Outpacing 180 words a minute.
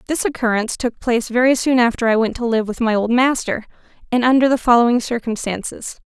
Yes: average, 200 wpm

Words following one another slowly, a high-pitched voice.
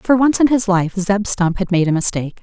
No: fast, 270 wpm; high, 200 Hz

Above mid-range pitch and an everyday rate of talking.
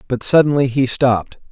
No: low, 130 Hz; average, 160 wpm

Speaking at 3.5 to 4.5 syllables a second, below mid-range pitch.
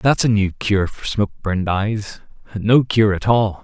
Yes: 4.4 syllables/s; low, 105 Hz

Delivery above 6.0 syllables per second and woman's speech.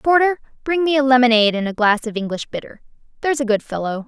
Yes: 6.8 syllables/s; female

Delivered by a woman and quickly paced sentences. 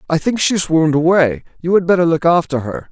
No: male; fast, 225 wpm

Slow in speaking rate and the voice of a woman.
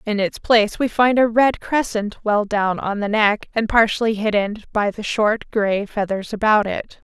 No: average, 195 wpm; female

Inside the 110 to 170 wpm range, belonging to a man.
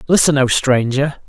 Yes: average, 140 wpm; male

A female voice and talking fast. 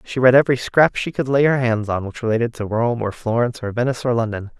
No: male; fast, 260 wpm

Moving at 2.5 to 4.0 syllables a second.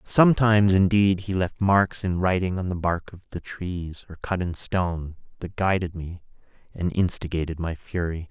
No: 4.8 syllables/s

